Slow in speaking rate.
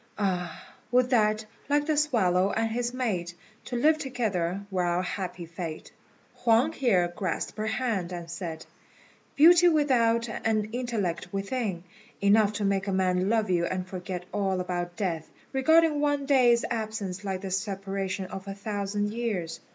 No: average, 155 wpm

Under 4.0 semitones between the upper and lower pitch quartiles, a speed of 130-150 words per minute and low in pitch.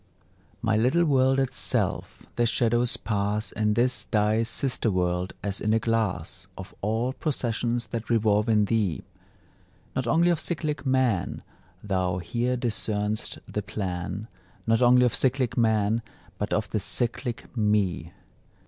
Yes: average, 3.0 semitones; average, 140 wpm; low, 110 Hz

